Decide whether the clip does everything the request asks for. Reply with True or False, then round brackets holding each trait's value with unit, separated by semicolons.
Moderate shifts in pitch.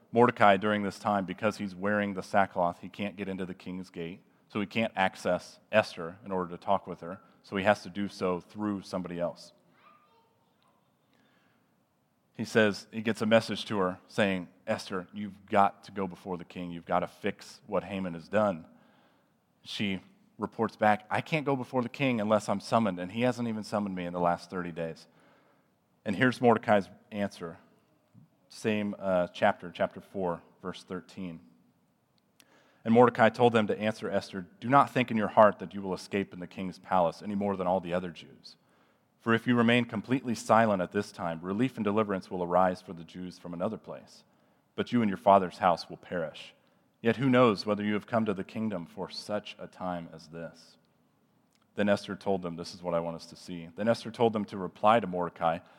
True (3.4 semitones)